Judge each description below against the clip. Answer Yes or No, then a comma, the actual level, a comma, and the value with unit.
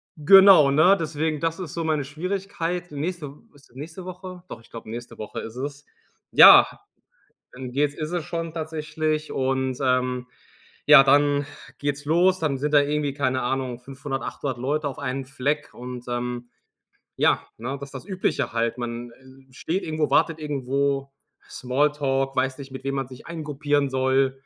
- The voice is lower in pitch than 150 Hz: Yes, medium, 140 Hz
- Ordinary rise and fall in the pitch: Yes, average, 3.0 semitones